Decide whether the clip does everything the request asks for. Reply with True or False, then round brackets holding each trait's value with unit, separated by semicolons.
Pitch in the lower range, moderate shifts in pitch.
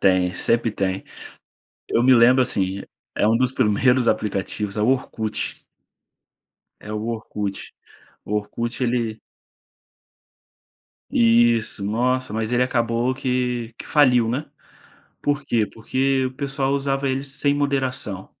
True (120 Hz; 3.2 semitones)